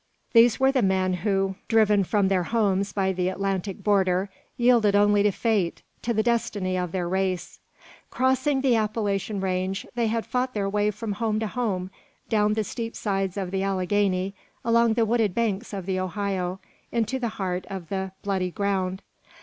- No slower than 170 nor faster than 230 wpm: Yes, average, 175 wpm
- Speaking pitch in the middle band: No, high, 200 Hz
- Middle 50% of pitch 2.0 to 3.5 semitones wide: Yes, average, 2.9 semitones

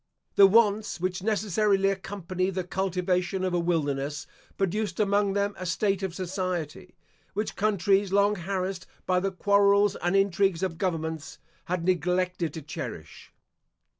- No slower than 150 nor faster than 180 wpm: No, slow, 135 wpm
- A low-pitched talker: No, high, 190 Hz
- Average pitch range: No, narrow, 2.2 semitones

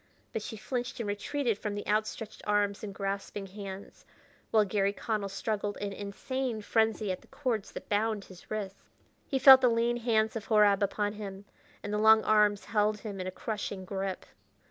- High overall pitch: Yes, high, 210 Hz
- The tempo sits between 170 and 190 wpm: Yes, average, 185 wpm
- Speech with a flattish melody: Yes, narrow, 1.7 semitones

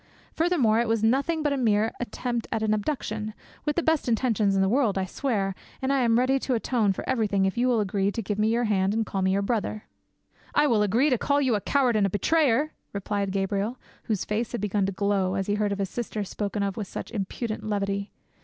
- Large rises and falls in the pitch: No, average, 3.7 semitones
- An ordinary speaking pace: No, fast, 235 wpm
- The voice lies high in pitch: Yes, high, 215 Hz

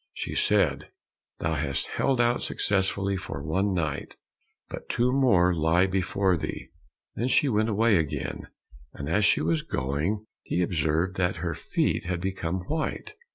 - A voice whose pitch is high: No, very low, 90 Hz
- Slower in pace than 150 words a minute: No, average, 155 wpm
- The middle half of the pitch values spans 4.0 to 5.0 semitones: Yes, average, 4.3 semitones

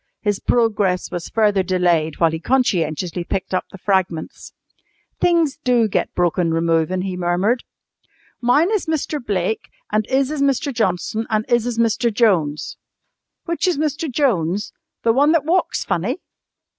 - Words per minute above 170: No, average, 150 wpm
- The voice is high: Yes, high, 215 Hz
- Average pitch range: No, wide, 6.6 semitones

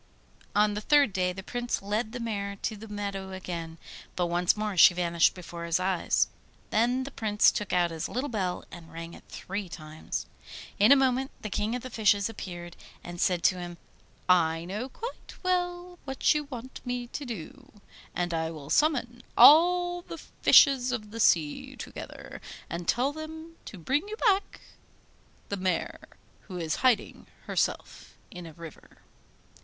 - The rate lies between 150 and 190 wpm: Yes, average, 170 wpm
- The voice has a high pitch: Yes, high, 210 Hz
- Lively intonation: Yes, wide, 6.7 semitones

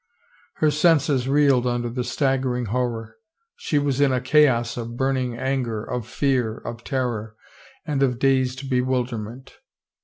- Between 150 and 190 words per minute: No, average, 140 wpm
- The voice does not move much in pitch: Yes, narrow, 2.3 semitones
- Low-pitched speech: Yes, low, 130 Hz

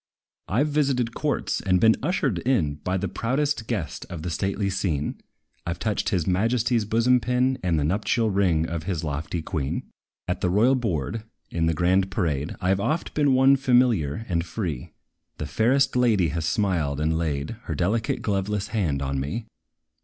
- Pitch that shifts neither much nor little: No, wide, 6.3 semitones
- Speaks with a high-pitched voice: No, very low, 95 Hz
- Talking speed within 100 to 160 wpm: No, average, 180 wpm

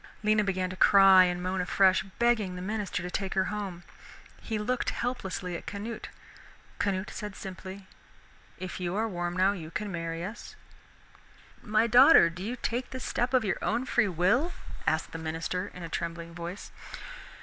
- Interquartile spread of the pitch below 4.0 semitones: Yes, average, 3.1 semitones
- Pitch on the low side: No, high, 190 Hz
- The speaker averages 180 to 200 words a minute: No, average, 170 wpm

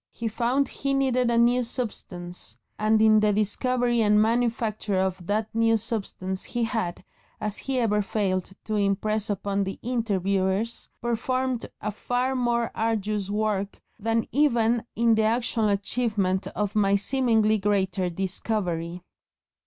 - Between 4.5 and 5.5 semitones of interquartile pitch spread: No, average, 3.0 semitones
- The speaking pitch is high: Yes, high, 215 Hz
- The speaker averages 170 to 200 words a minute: No, slow, 135 wpm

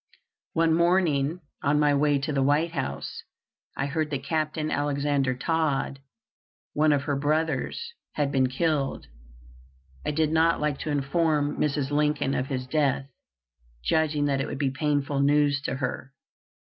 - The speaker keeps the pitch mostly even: Yes, narrow, 2.1 semitones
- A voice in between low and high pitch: Yes, medium, 145 Hz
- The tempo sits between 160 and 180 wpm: No, average, 150 wpm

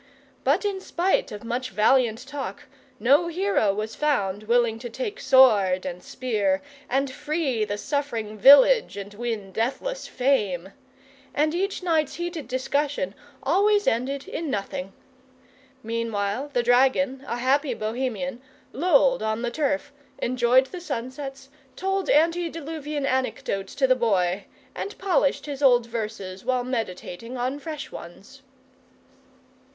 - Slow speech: Yes, slow, 130 wpm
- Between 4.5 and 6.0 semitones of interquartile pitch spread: Yes, average, 4.8 semitones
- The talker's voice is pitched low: No, very high, 260 Hz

